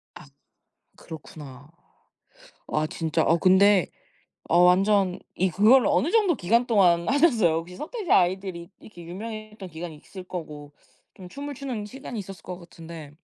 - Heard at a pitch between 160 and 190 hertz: Yes, medium, 185 Hz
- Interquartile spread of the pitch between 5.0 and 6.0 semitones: No, average, 4.5 semitones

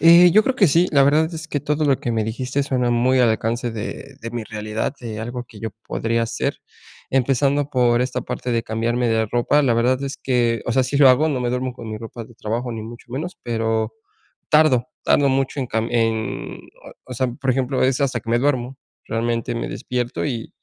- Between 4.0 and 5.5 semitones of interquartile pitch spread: No, average, 2.8 semitones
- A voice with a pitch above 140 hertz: No, low, 125 Hz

